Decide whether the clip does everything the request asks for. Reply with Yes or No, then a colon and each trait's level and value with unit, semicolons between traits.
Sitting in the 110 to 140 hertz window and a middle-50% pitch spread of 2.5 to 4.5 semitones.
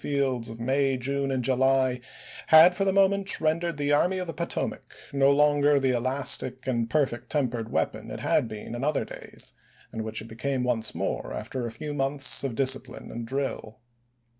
Yes: low, 135 Hz; average, 3.2 semitones